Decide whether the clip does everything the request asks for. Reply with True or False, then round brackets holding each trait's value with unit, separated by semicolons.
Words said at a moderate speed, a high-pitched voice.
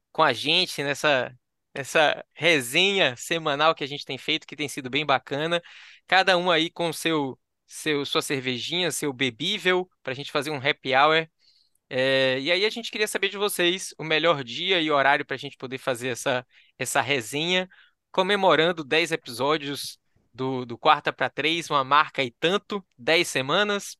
False (175 wpm; 150 Hz)